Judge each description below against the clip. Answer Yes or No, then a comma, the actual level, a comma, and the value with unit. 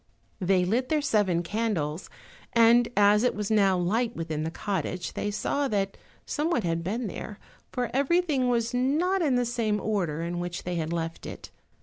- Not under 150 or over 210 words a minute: Yes, average, 180 wpm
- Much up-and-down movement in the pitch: Yes, wide, 5.8 semitones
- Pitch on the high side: Yes, high, 210 Hz